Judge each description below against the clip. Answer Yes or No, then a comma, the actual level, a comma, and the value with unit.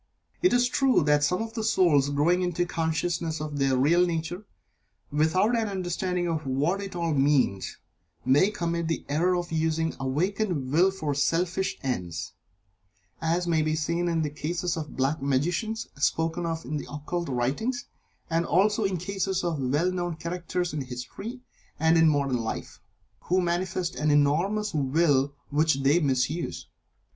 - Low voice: No, medium, 165 Hz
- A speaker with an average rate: Yes, average, 165 wpm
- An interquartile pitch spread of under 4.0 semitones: Yes, average, 3.6 semitones